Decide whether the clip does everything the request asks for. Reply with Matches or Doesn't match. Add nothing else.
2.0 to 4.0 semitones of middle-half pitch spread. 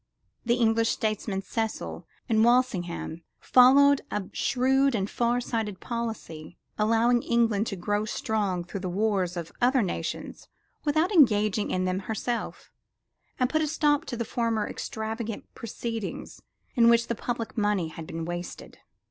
Matches